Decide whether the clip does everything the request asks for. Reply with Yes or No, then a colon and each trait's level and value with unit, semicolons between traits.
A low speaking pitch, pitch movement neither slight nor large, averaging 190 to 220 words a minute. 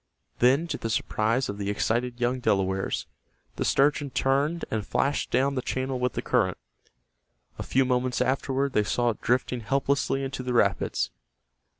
No: low, 125 Hz; average, 3.3 semitones; average, 165 wpm